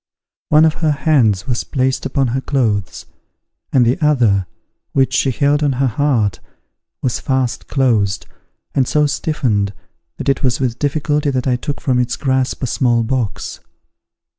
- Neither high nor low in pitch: No, low, 130 Hz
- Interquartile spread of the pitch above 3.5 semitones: No, average, 3.2 semitones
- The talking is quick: No, average, 160 wpm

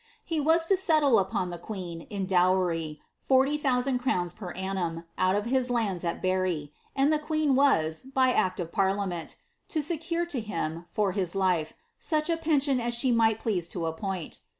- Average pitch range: No, wide, 7.5 semitones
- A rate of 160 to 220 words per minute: Yes, average, 175 wpm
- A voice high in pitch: Yes, high, 205 Hz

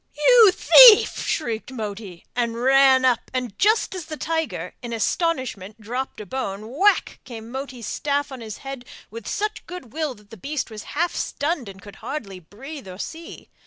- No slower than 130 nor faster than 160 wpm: No, average, 175 wpm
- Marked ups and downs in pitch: Yes, wide, 5.9 semitones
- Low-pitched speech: No, very high, 260 Hz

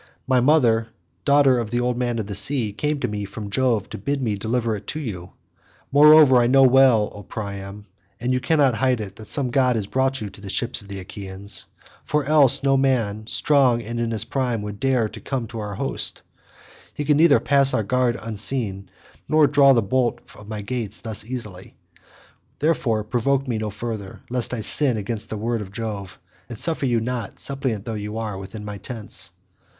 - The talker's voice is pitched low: Yes, low, 115 Hz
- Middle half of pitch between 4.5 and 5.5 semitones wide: No, average, 4.1 semitones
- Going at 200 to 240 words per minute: Yes, fast, 205 wpm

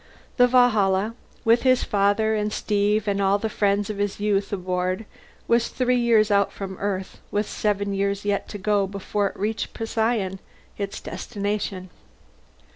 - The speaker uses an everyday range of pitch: No, narrow, 1.8 semitones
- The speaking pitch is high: Yes, high, 205 Hz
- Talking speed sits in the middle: Yes, average, 155 wpm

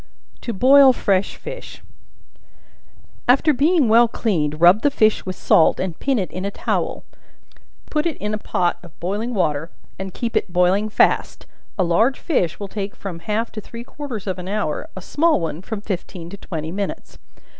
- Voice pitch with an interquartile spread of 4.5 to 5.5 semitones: Yes, average, 4.9 semitones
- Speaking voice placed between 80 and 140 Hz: No, high, 205 Hz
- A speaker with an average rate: Yes, average, 180 wpm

